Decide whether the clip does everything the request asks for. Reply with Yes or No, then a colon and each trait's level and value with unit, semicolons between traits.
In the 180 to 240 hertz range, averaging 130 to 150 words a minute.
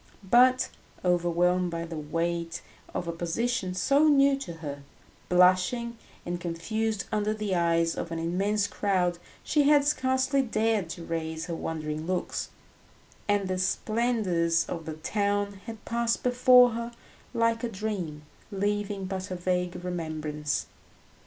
Yes: medium, 185 Hz; average, 140 wpm